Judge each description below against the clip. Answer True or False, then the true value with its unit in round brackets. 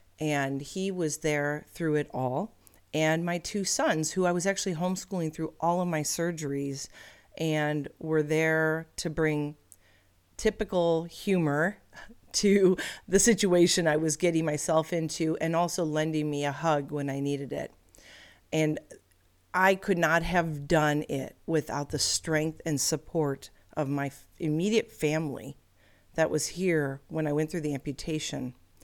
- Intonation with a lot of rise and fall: False (2.9 semitones)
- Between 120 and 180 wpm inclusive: True (150 wpm)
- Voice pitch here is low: False (155 Hz)